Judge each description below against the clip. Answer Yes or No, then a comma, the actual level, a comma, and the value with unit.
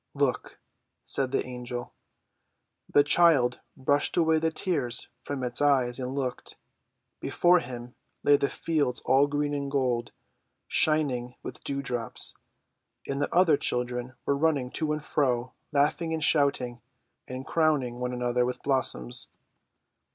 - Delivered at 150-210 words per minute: No, slow, 135 wpm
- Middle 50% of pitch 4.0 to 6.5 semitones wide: No, average, 3.0 semitones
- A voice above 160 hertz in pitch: No, low, 135 Hz